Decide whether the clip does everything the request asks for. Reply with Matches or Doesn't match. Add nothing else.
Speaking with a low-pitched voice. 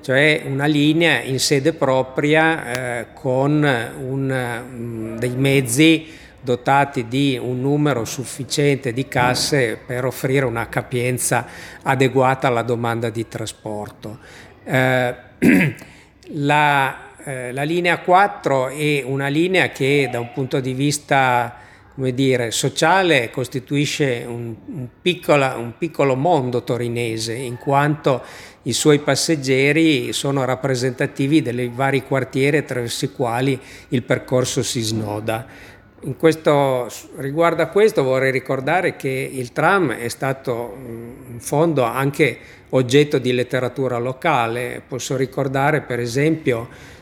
Matches